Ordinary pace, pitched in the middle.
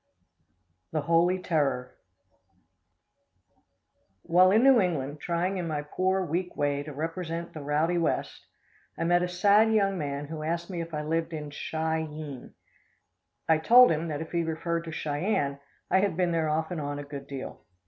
Yes: average, 175 wpm; medium, 165 Hz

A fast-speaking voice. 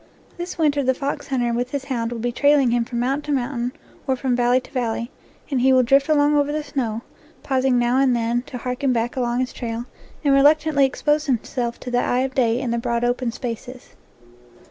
Yes: fast, 215 wpm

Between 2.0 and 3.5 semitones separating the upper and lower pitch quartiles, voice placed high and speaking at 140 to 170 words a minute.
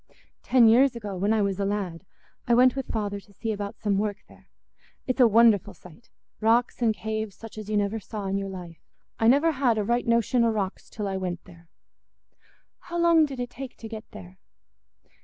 No: average, 3.2 semitones; high, 215 Hz; fast, 205 wpm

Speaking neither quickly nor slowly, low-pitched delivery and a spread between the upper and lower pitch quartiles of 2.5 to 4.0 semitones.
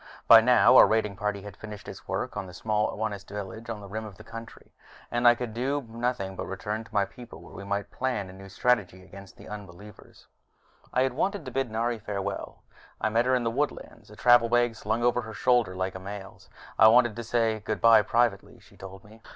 No: fast, 225 wpm; low, 110 Hz; average, 3.1 semitones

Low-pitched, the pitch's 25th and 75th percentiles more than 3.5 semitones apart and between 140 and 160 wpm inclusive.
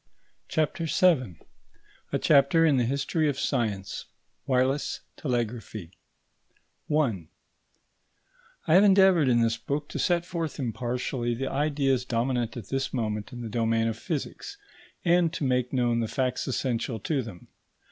Yes: low, 130 Hz; average, 4.4 semitones; average, 145 wpm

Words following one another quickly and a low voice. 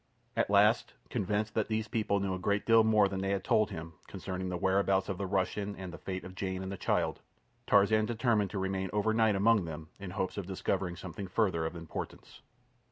Yes: fast, 215 wpm; low, 100 Hz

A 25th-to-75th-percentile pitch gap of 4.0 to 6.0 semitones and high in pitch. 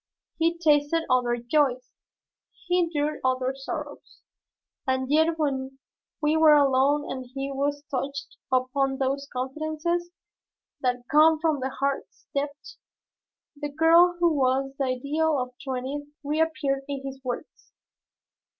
No: average, 2.8 semitones; very high, 280 Hz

